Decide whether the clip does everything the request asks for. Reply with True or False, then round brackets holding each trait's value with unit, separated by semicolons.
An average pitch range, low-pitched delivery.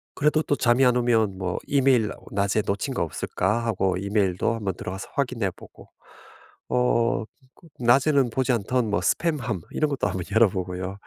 True (4.6 semitones; 115 Hz)